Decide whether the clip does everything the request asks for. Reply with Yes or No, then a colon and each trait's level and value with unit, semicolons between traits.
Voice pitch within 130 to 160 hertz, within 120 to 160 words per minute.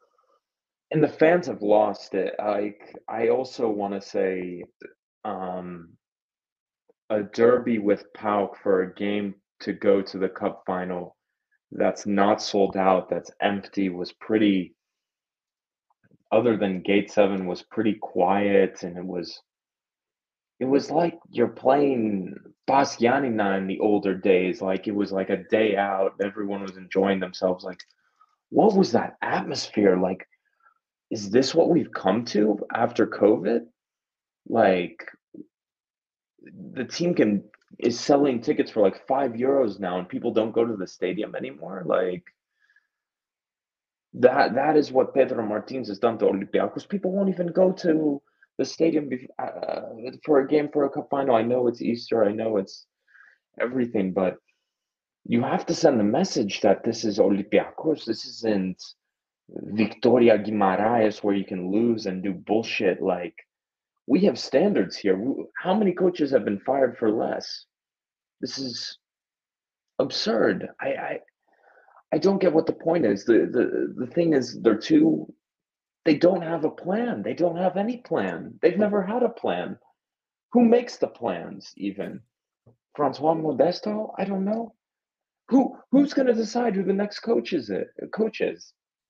No: low, 120 Hz; average, 150 wpm